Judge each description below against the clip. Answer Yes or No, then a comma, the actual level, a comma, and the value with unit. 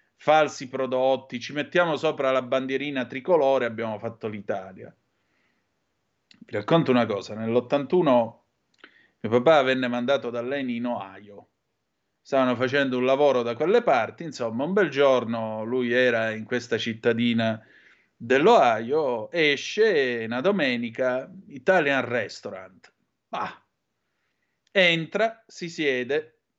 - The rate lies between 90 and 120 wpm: Yes, slow, 115 wpm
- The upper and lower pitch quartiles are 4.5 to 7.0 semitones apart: Yes, average, 5.2 semitones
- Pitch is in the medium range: No, low, 130 Hz